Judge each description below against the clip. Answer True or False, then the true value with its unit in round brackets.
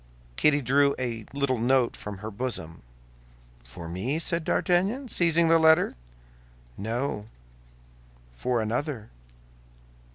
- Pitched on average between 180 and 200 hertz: False (130 Hz)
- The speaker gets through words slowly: True (105 wpm)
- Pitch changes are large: True (6.5 semitones)